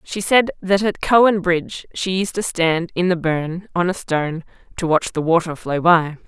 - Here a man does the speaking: No, female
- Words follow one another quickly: Yes, fast, 210 wpm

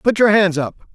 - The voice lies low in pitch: No, high, 190 Hz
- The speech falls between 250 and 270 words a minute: Yes, fast, 255 wpm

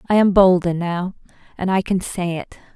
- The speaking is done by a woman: Yes, female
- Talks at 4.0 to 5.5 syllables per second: Yes, 5.1 syllables/s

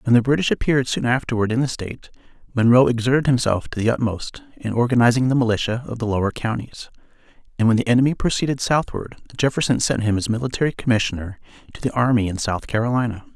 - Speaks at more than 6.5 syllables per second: Yes, 6.7 syllables/s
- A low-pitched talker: Yes, low, 120 Hz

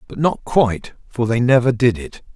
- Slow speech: No, fast, 205 wpm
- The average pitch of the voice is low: Yes, low, 120 Hz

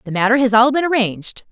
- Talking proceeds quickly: Yes, fast, 240 wpm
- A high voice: Yes, high, 240 Hz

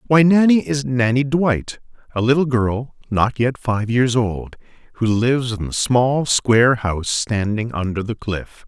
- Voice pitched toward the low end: Yes, low, 120 Hz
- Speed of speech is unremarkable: Yes, average, 160 wpm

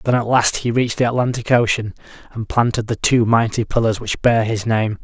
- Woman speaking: No, male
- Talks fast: Yes, fast, 215 wpm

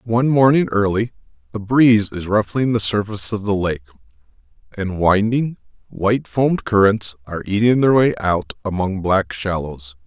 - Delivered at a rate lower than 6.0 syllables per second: Yes, 5.1 syllables/s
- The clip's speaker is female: No, male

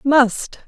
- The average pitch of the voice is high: Yes, very high, 250 Hz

